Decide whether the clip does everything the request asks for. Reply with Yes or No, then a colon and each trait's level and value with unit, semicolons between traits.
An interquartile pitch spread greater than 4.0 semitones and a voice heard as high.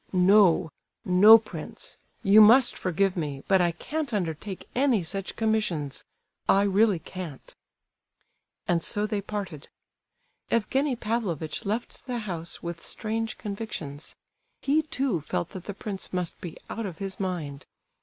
Yes: average, 4.5 semitones; high, 195 Hz